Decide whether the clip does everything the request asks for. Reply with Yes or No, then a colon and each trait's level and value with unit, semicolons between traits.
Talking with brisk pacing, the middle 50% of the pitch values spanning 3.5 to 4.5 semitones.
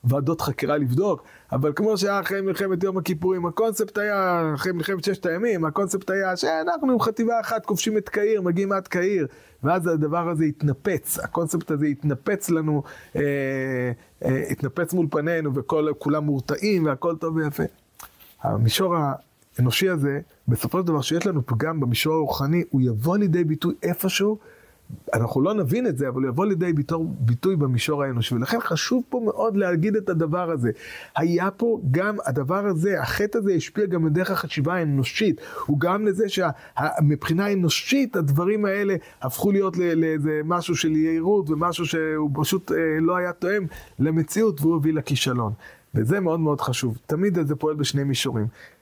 No: fast, 155 wpm; average, 4.9 semitones